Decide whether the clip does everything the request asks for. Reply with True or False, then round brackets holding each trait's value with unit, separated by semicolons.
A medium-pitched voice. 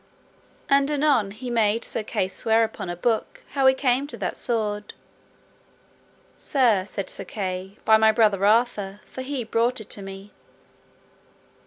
False (220 Hz)